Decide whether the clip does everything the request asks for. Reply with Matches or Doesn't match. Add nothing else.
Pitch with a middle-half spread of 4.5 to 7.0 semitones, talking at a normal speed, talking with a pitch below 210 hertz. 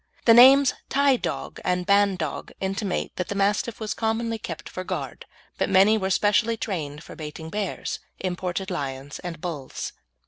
Doesn't match